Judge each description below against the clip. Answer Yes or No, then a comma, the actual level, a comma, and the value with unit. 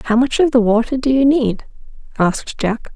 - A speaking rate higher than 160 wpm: Yes, fast, 205 wpm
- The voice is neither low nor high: No, high, 240 Hz